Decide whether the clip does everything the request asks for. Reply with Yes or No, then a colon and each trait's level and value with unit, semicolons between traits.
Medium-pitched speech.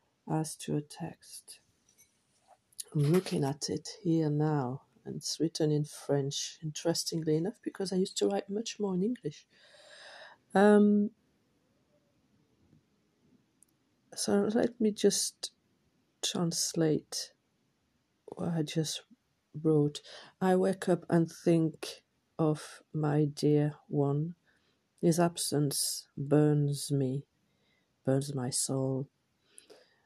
Yes: medium, 155 Hz